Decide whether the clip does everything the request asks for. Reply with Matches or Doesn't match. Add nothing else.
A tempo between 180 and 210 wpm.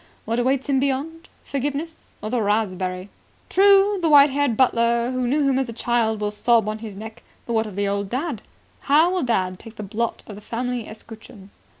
Matches